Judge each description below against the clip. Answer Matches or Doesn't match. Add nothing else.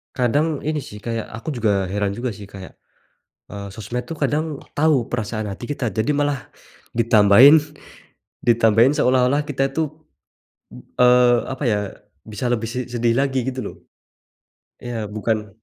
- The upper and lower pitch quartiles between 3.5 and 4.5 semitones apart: Matches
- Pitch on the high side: Doesn't match